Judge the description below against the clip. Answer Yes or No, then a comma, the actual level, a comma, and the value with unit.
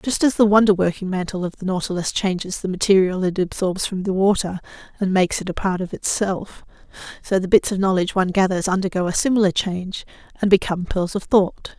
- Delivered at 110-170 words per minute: No, fast, 205 wpm